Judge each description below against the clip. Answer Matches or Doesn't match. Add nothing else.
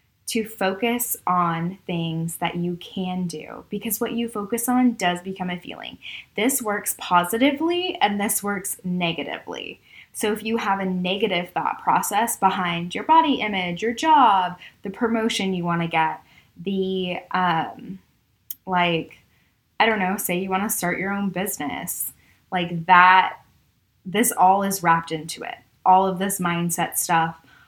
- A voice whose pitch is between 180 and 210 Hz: Matches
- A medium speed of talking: Matches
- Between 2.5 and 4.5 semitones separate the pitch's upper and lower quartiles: Matches